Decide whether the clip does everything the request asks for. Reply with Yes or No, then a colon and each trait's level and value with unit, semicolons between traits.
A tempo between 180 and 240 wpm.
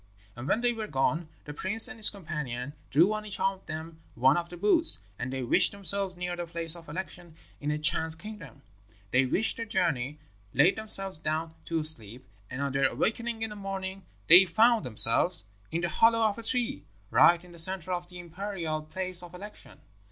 Yes: average, 200 wpm